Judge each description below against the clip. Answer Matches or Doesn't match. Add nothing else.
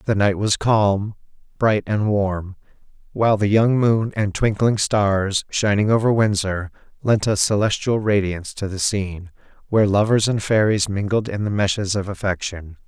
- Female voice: Doesn't match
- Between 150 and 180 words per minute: Matches